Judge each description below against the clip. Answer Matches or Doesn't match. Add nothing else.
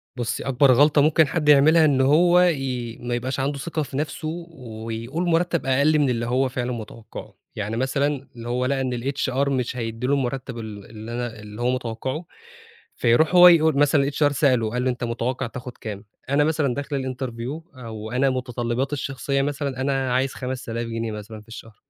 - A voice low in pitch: Matches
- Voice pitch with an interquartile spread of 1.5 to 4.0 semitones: Matches